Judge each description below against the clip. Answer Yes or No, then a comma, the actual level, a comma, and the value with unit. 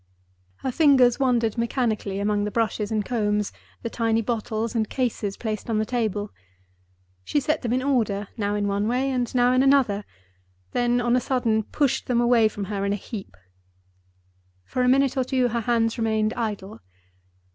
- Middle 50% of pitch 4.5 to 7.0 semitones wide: No, average, 3.1 semitones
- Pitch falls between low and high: No, high, 225 Hz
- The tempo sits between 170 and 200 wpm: Yes, average, 175 wpm